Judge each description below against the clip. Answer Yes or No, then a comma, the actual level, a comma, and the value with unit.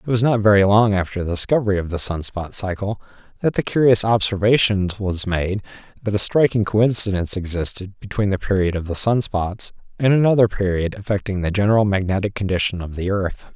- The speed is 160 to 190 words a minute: Yes, average, 185 wpm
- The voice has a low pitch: Yes, low, 100 Hz